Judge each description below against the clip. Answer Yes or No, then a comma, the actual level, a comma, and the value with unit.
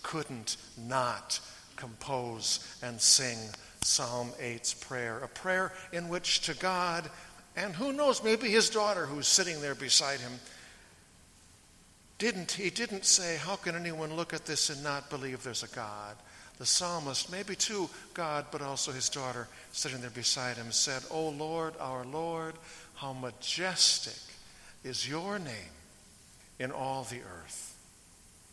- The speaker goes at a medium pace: Yes, average, 145 wpm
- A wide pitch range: Yes, wide, 5.9 semitones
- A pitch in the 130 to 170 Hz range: Yes, medium, 140 Hz